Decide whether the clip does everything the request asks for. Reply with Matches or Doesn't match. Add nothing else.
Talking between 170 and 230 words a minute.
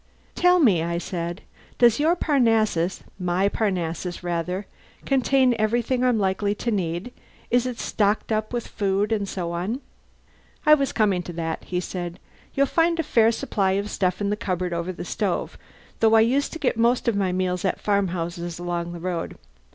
Matches